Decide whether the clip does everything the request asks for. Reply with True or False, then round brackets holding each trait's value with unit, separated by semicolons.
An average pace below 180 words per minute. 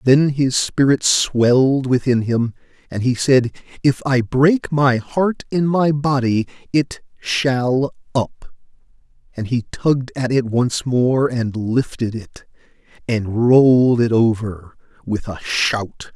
True (135 wpm)